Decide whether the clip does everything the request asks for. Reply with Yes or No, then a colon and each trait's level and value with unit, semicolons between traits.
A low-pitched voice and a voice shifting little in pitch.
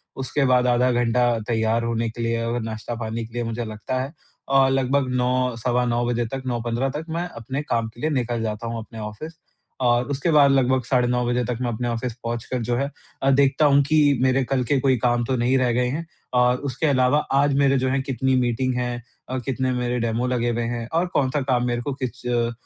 Yes: low, 125 Hz; narrow, 2.1 semitones